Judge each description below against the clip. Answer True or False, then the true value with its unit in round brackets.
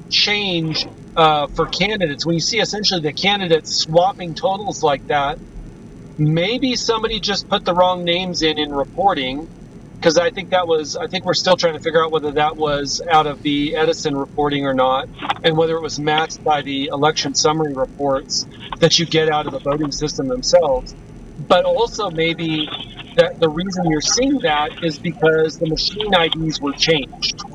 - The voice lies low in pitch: False (160 Hz)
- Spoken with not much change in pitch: False (3.2 semitones)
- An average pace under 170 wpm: False (180 wpm)